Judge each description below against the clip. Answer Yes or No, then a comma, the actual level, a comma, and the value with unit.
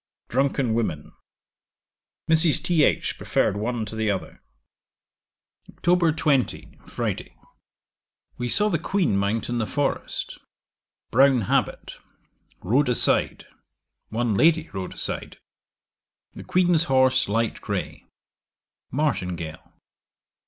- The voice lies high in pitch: No, low, 125 Hz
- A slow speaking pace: Yes, slow, 100 wpm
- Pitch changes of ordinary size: No, wide, 6.1 semitones